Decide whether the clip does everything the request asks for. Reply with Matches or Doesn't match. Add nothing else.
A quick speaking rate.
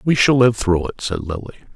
Matches